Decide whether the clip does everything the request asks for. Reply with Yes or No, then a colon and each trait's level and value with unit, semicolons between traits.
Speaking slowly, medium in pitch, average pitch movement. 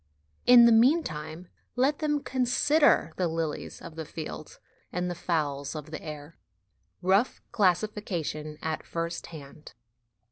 No: slow, 130 wpm; medium, 170 Hz; wide, 7.2 semitones